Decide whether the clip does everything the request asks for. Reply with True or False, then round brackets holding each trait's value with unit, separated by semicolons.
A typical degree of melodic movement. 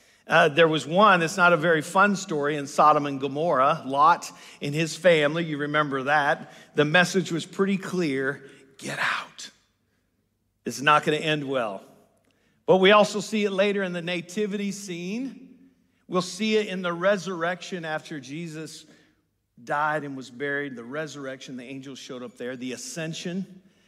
True (4.9 semitones)